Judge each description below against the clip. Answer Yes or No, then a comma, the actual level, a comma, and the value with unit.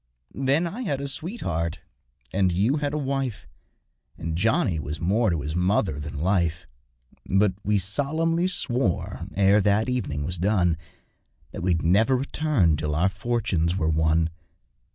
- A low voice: Yes, very low, 95 Hz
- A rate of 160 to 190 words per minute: No, average, 150 wpm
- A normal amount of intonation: No, wide, 8.0 semitones